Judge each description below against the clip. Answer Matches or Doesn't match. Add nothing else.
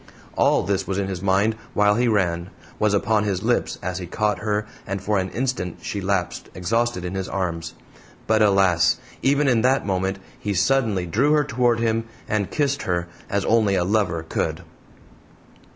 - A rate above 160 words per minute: Matches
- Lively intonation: Doesn't match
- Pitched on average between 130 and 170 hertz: Doesn't match